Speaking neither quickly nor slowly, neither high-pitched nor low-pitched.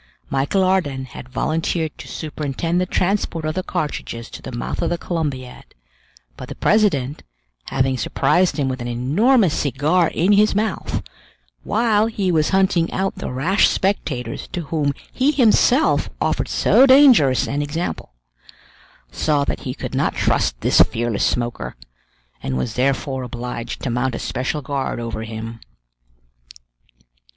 Yes: average, 145 wpm; medium, 150 Hz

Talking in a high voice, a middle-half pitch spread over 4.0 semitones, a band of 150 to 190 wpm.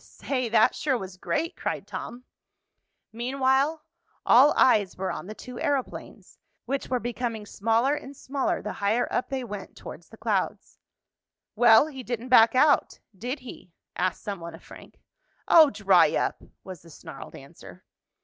Yes: high, 245 Hz; average, 4.5 semitones; average, 160 wpm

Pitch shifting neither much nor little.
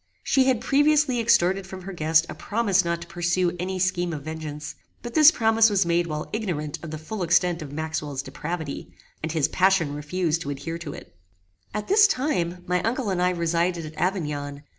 Yes: average, 3.8 semitones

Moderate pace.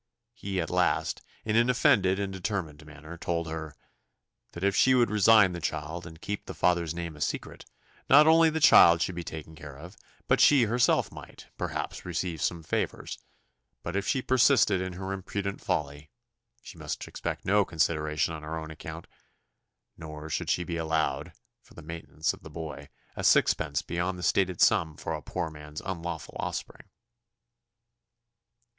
Yes: average, 170 wpm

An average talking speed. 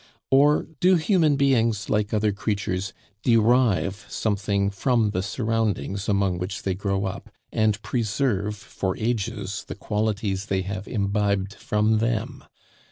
No: slow, 130 wpm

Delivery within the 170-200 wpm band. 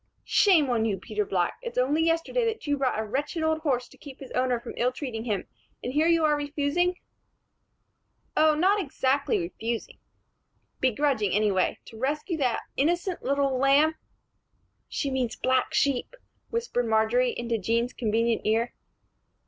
No: average, 160 wpm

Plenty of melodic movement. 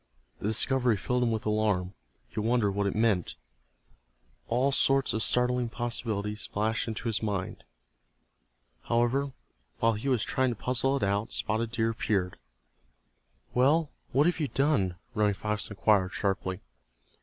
No: average, 3.2 semitones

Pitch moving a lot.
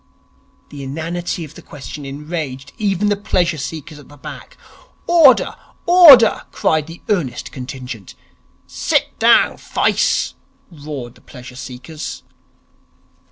No: average, 4.7 semitones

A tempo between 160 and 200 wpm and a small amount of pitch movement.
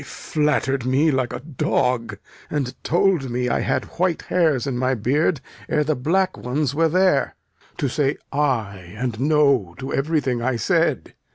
No: average, 165 wpm; average, 3.7 semitones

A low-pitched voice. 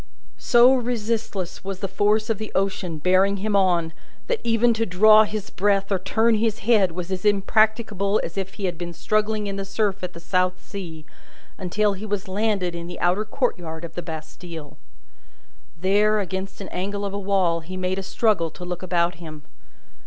No: high, 195 Hz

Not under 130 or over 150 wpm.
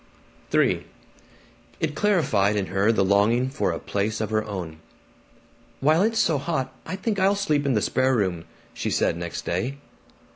No: average, 170 wpm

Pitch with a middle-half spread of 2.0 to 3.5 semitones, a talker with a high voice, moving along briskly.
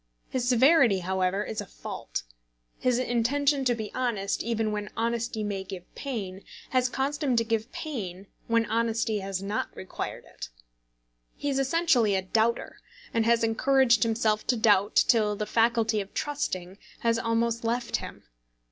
No: average, 3.0 semitones; high, 230 Hz; average, 155 wpm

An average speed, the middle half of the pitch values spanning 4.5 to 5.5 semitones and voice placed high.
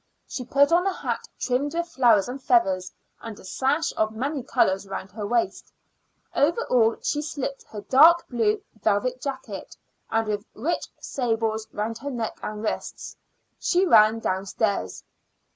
Yes: average, 155 wpm; average, 4.9 semitones; high, 235 Hz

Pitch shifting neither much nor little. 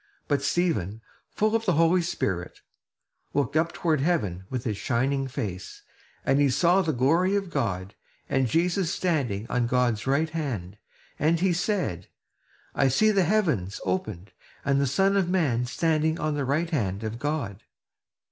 No: wide, 6.9 semitones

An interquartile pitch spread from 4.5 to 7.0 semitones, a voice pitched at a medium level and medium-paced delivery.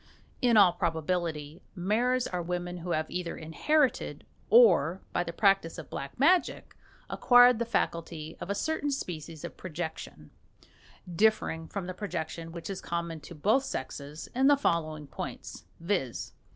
Yes: average, 5.2 semitones; medium, 175 Hz; average, 150 wpm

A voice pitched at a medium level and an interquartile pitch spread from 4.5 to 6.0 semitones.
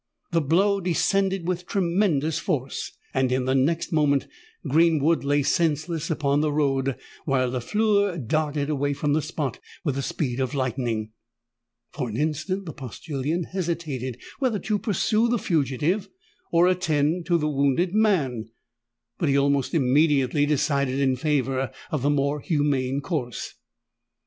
No: medium, 150 Hz; average, 3.9 semitones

